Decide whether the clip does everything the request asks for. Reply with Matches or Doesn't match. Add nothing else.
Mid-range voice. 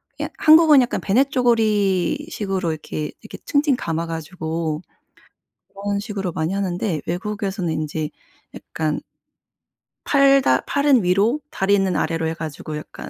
Doesn't match